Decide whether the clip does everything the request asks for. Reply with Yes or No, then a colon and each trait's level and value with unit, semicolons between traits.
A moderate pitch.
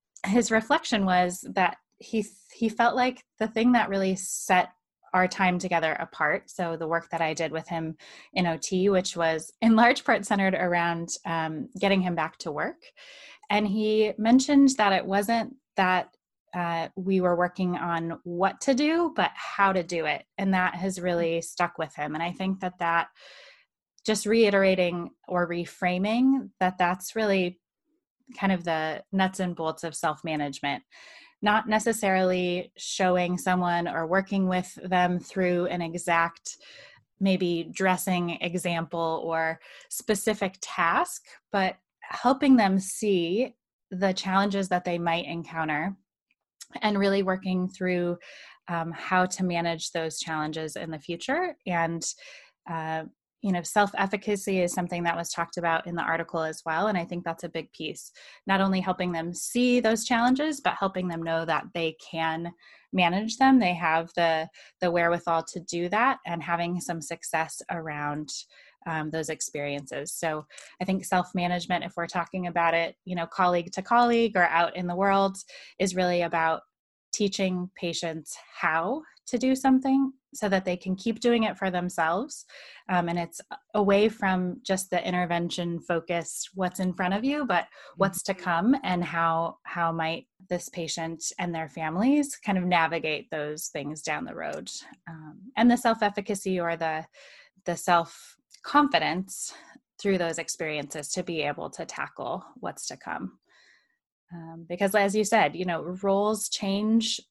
Yes: medium, 180 Hz